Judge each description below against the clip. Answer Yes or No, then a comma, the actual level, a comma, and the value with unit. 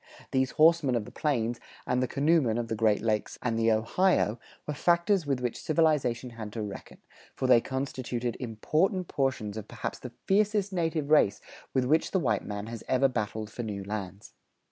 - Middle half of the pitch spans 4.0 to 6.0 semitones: Yes, wide, 5.6 semitones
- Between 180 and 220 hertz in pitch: No, low, 125 Hz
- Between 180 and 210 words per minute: Yes, average, 185 wpm